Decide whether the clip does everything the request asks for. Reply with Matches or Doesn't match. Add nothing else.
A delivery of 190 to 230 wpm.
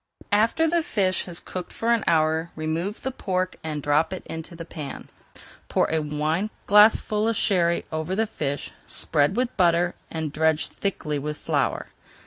Doesn't match